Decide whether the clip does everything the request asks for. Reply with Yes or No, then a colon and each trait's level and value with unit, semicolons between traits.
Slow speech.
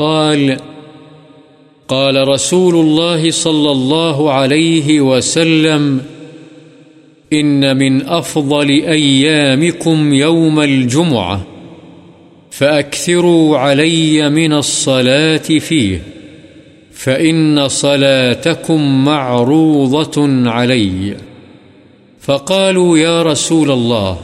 Yes: slow, 65 wpm